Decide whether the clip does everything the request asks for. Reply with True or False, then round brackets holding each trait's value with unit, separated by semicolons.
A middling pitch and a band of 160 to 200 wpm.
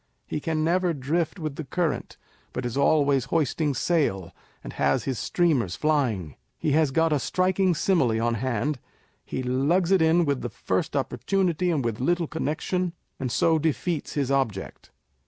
True (150 Hz; 165 wpm)